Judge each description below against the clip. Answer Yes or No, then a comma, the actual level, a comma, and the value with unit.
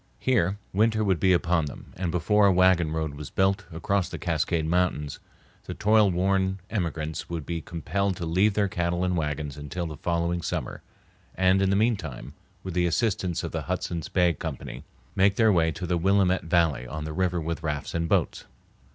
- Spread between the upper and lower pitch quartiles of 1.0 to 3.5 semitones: Yes, average, 2.9 semitones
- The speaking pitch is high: No, very low, 85 Hz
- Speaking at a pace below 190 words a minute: No, average, 195 wpm